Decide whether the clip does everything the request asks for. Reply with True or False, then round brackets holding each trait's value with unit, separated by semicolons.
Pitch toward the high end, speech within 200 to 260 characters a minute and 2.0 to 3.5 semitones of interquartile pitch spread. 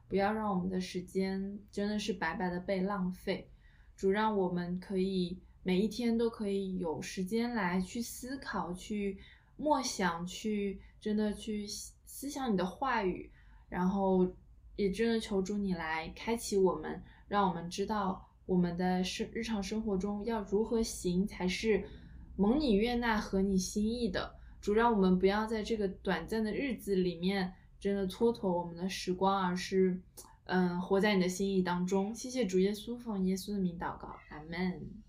True (195 Hz; 240 characters per minute; 2.7 semitones)